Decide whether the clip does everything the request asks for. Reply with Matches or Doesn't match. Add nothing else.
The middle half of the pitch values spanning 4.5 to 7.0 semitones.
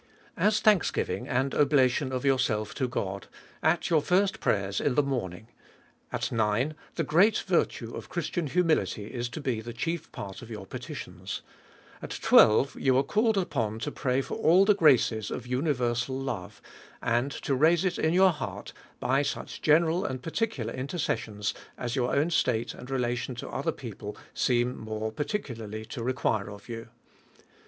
Matches